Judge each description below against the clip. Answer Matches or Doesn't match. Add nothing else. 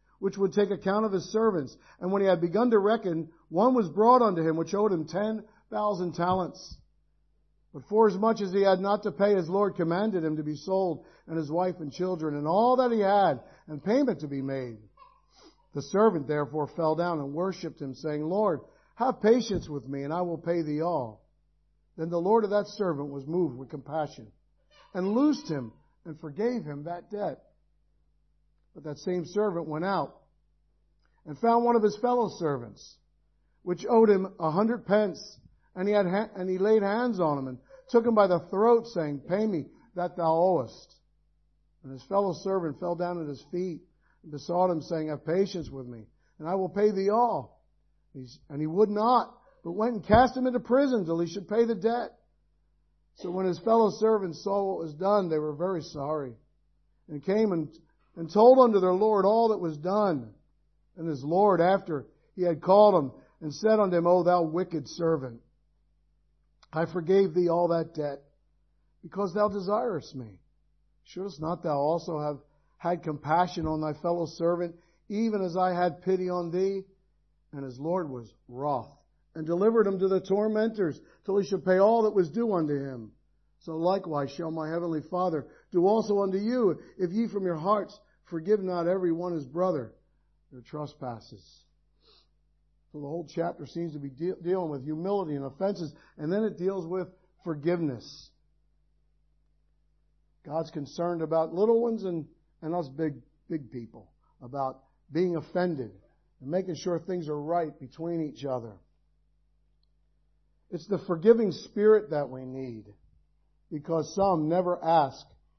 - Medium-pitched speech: Matches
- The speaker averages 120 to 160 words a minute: Doesn't match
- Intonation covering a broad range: Doesn't match